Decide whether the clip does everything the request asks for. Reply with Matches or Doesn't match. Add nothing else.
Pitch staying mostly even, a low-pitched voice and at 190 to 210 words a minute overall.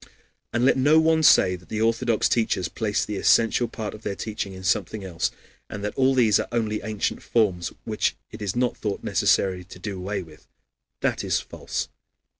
Doesn't match